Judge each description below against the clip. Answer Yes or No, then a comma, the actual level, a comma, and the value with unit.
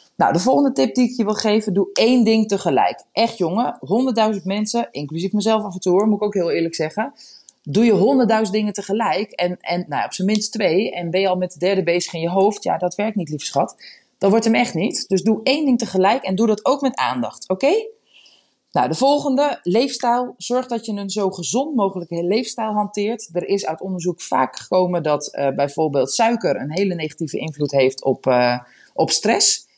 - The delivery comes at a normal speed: No, fast, 215 wpm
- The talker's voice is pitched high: Yes, high, 200 Hz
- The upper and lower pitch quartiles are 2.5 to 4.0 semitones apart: No, average, 4.6 semitones